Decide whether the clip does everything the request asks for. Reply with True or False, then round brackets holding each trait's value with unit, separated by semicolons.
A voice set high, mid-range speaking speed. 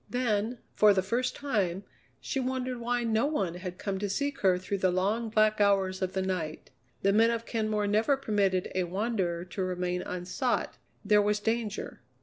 True (205 Hz; 180 wpm)